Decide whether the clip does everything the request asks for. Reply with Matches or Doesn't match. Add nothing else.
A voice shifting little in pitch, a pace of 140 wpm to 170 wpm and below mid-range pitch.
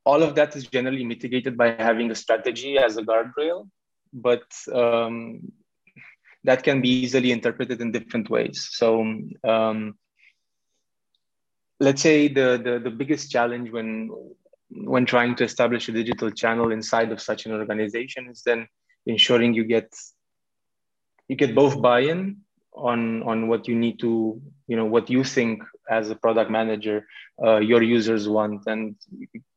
Matches